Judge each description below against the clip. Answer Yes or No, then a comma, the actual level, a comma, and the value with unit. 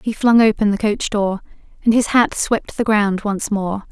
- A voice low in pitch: No, high, 210 Hz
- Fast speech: Yes, fast, 215 wpm